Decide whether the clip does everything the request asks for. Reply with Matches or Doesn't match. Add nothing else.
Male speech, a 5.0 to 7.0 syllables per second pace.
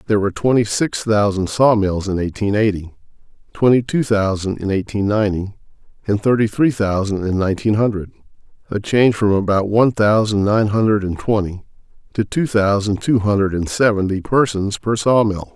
Matches